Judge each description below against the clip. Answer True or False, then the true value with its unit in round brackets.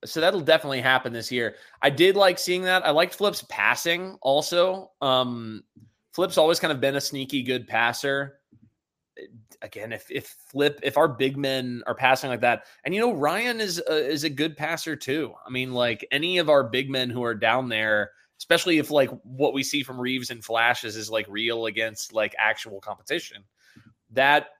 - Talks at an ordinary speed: True (195 wpm)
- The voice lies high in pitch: False (135 Hz)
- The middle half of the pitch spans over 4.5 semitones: True (4.9 semitones)